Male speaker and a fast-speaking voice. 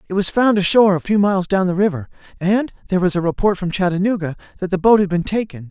Yes: male; fast, 240 wpm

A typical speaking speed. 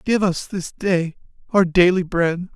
Yes: average, 165 wpm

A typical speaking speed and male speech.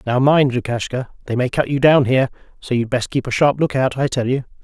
No: fast, 245 wpm; male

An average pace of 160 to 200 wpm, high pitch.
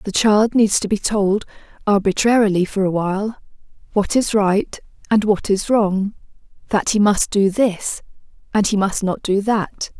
Yes: average, 170 wpm; high, 205 Hz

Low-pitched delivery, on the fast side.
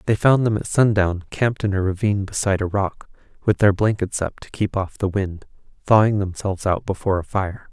Yes: low, 100 Hz; fast, 210 wpm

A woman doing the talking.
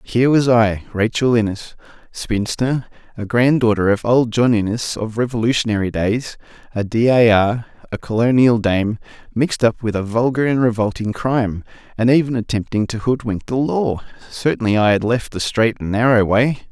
No: male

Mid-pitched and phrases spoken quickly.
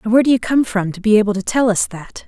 No: high, 215 Hz; fast, 340 wpm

